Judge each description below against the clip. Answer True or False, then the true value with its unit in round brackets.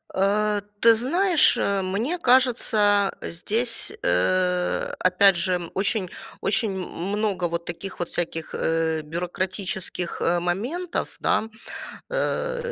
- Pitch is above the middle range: True (195 Hz)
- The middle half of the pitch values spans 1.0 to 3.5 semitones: False (4.5 semitones)